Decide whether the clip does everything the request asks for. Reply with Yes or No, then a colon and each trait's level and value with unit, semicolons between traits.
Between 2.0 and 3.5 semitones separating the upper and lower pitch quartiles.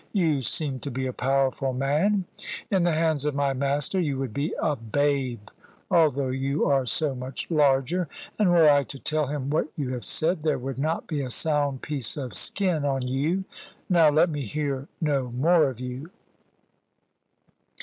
Yes: average, 2.9 semitones